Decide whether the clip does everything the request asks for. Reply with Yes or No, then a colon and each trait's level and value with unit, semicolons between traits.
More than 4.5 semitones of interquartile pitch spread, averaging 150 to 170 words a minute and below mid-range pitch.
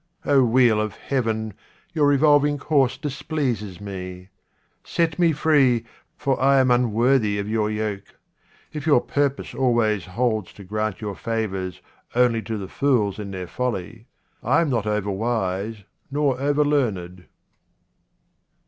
No: average, 5.0 semitones; average, 140 wpm; low, 115 Hz